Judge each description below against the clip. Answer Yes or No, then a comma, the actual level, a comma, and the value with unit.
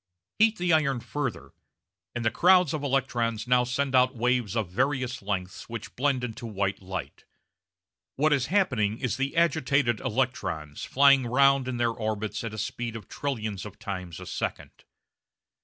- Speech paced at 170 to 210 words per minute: No, average, 160 wpm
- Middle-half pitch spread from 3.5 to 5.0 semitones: Yes, average, 4.4 semitones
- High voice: No, low, 125 Hz